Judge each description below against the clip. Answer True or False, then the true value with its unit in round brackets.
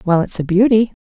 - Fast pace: True (230 wpm)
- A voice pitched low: False (200 Hz)